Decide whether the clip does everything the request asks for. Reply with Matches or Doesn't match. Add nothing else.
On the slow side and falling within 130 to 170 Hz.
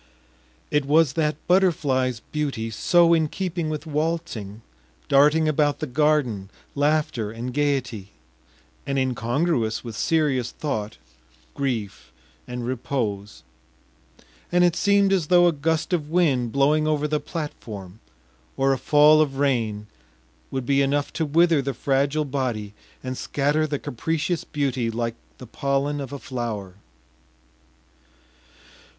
Matches